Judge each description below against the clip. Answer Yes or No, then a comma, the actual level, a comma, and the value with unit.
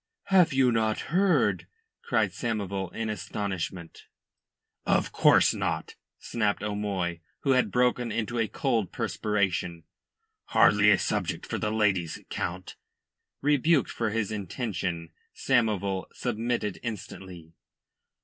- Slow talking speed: Yes, slow, 110 wpm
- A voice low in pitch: Yes, low, 105 Hz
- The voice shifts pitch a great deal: No, average, 4.0 semitones